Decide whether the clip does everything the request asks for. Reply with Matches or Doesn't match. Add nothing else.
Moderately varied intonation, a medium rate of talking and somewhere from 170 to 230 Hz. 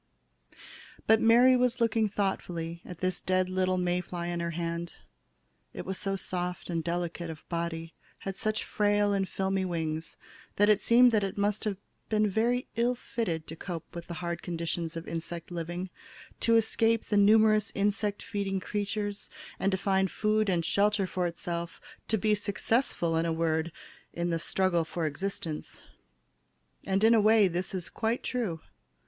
Matches